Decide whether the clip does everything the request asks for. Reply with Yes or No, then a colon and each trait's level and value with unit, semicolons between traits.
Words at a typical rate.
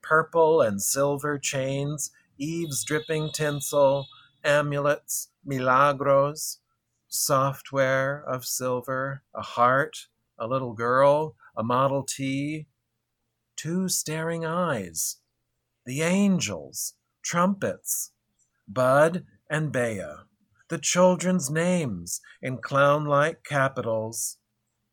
No: slow, 85 wpm